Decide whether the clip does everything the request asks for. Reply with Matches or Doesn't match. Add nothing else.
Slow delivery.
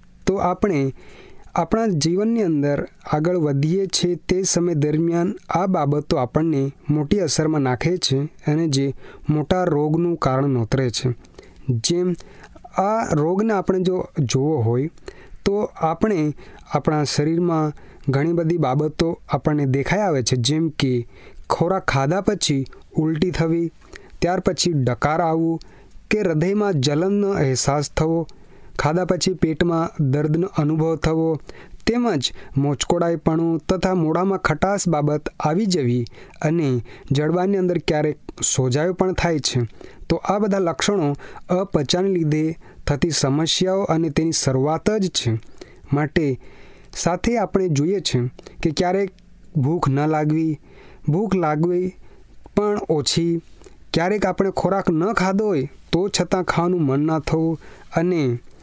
Doesn't match